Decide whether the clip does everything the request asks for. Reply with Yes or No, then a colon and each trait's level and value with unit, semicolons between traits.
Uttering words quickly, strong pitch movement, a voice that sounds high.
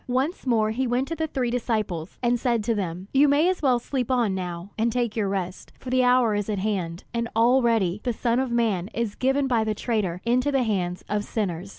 No: fast, 230 wpm; average, 3.9 semitones; high, 230 Hz